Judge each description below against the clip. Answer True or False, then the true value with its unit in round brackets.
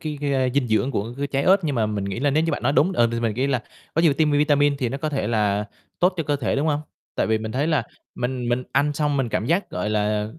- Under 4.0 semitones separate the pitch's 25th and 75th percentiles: False (4.8 semitones)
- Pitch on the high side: False (135 Hz)